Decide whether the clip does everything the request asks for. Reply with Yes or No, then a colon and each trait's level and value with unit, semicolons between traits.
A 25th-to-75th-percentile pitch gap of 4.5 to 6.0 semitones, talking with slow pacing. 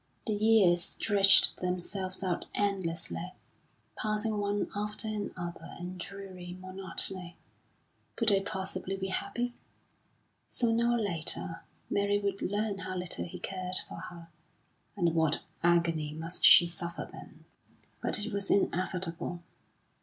No: average, 2.8 semitones; slow, 125 wpm